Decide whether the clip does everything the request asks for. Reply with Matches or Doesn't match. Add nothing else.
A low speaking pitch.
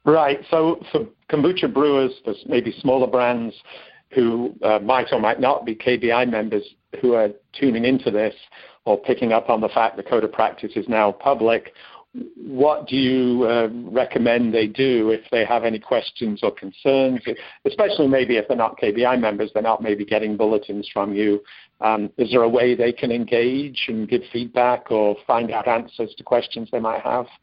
Matches